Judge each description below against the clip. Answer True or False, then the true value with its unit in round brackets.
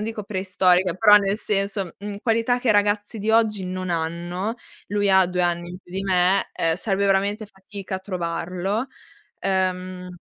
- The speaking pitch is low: False (195 Hz)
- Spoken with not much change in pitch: True (2.2 semitones)